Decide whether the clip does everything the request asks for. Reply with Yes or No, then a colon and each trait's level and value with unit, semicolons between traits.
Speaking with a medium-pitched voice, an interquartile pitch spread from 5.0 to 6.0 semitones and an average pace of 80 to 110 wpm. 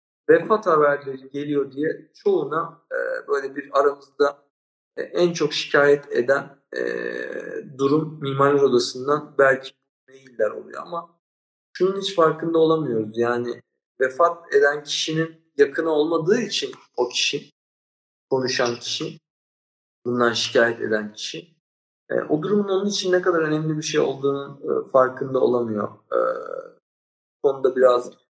No: medium, 150 Hz; wide, 5.5 semitones; average, 125 wpm